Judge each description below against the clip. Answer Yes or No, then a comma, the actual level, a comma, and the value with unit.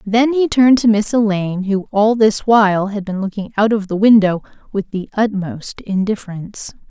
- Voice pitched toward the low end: No, high, 205 Hz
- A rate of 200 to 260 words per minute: No, average, 180 wpm